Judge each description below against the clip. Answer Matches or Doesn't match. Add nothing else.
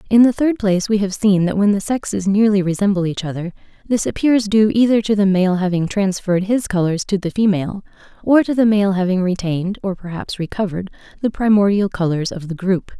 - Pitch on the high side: Matches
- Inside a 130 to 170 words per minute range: Doesn't match